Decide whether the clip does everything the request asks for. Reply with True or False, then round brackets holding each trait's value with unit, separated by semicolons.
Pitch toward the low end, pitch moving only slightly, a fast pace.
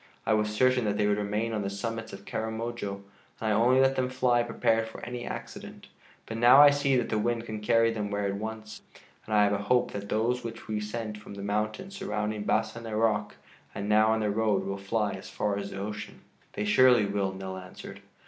True (110 Hz; 2.1 semitones; 225 wpm)